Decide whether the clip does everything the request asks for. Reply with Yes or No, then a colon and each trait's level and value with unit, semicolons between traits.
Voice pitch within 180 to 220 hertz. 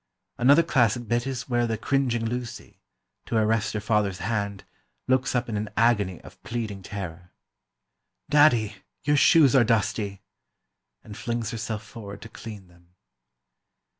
No: low, 115 Hz